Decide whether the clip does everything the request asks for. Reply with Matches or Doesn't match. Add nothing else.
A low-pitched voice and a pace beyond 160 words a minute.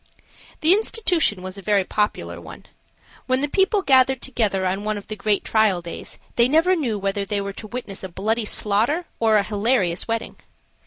Doesn't match